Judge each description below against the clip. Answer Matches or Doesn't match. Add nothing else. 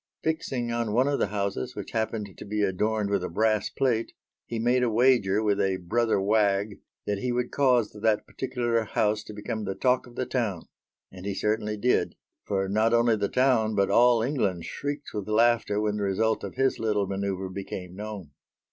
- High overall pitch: Doesn't match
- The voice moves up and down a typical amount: Matches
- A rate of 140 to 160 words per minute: Doesn't match